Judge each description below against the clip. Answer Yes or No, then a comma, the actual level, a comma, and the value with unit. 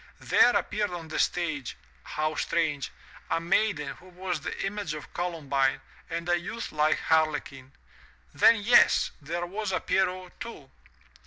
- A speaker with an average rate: Yes, average, 160 wpm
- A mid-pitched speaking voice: Yes, medium, 170 Hz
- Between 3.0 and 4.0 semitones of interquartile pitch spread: Yes, average, 3.6 semitones